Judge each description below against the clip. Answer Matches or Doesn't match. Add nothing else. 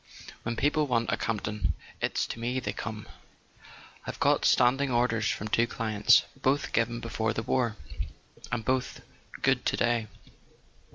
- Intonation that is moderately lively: Doesn't match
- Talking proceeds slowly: Doesn't match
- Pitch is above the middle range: Doesn't match